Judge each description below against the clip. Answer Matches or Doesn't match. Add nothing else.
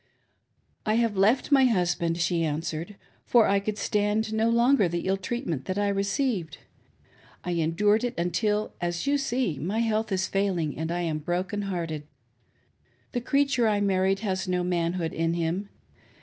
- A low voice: Doesn't match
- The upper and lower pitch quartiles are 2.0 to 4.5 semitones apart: Matches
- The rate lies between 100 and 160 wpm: Doesn't match